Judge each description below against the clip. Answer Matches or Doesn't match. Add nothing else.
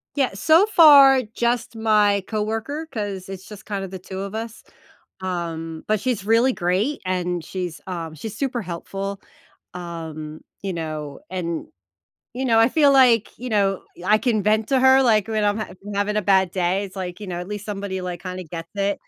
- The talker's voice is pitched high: Matches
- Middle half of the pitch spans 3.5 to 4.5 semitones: Matches